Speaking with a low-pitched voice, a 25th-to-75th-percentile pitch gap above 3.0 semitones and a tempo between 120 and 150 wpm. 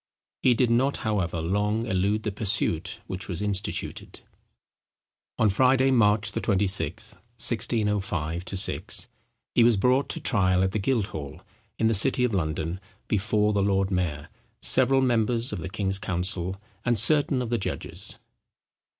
Yes: low, 105 Hz; average, 3.9 semitones; average, 140 wpm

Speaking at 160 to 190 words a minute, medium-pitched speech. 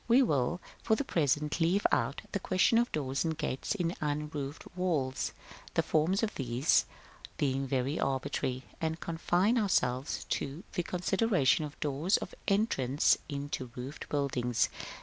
No: average, 145 wpm; medium, 150 Hz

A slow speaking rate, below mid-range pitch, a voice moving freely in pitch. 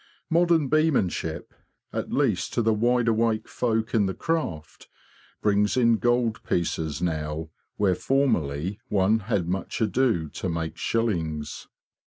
Yes: slow, 130 wpm; low, 105 Hz; wide, 6.2 semitones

